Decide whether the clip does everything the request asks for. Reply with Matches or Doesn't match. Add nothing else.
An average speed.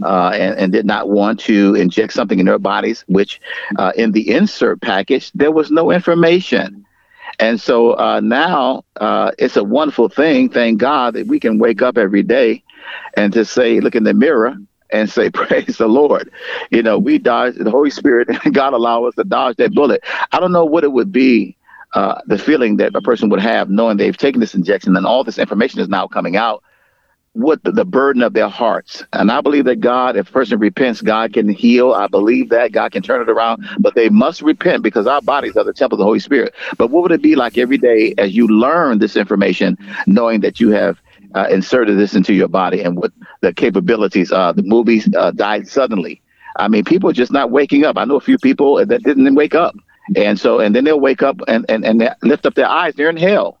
Doesn't match